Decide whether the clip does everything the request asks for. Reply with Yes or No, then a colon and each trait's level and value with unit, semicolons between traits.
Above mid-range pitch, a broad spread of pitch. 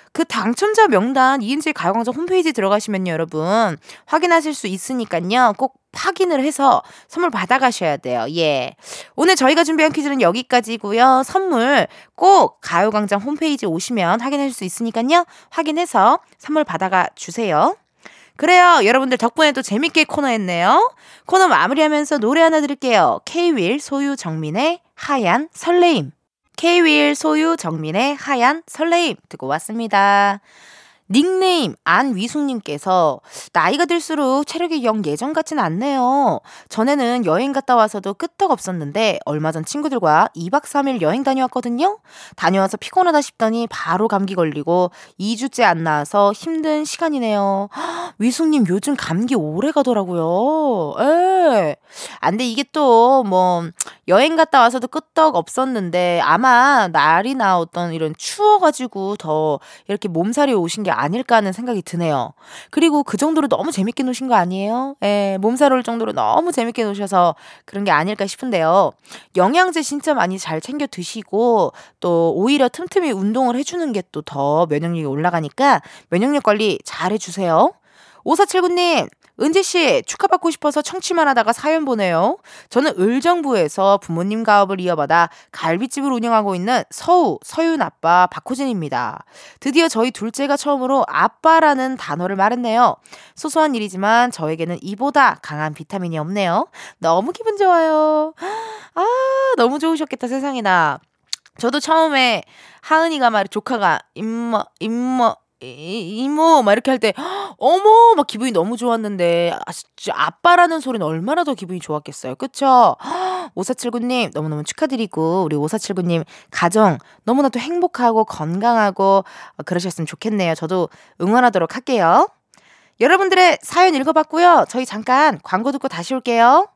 Yes: high, 245 Hz; wide, 7.9 semitones